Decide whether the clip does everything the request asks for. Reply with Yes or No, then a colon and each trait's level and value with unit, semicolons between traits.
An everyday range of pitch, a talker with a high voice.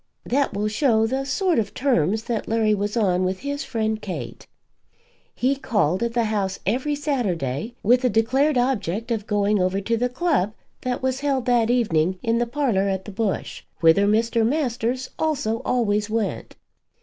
Yes: average, 3.8 semitones; high, 225 Hz